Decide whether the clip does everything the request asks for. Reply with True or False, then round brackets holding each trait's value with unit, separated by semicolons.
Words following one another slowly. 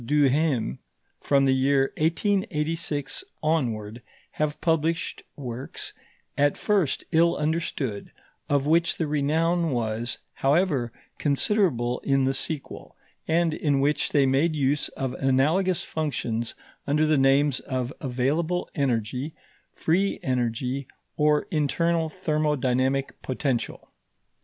True (110 wpm)